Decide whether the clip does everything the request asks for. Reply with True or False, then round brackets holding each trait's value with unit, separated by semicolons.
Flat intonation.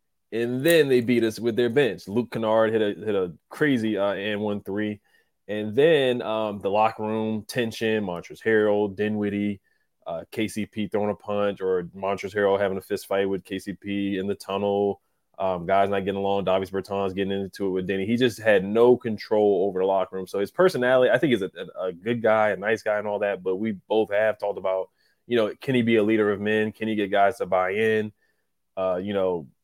True (2.0 semitones)